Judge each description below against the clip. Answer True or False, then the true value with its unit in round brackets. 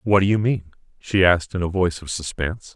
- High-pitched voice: False (90 Hz)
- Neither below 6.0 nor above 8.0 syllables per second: True (6.5 syllables/s)